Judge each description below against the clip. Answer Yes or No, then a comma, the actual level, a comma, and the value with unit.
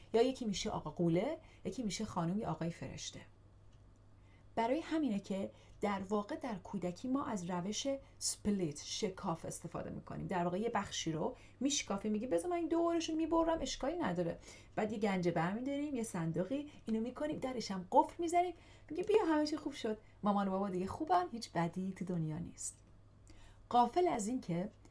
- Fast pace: Yes, fast, 170 wpm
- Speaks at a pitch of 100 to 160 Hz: No, high, 210 Hz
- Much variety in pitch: Yes, wide, 8.0 semitones